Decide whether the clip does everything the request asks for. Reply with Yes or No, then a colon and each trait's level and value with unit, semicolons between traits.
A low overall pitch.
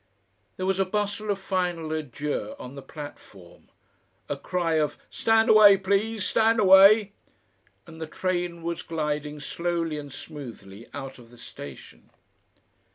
No: medium, 170 Hz